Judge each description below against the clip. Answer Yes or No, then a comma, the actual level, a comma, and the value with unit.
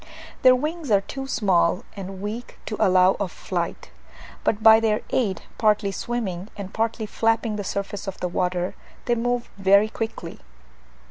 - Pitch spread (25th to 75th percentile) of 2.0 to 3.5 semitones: Yes, average, 3.1 semitones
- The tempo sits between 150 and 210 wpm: Yes, average, 155 wpm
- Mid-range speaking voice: No, high, 210 Hz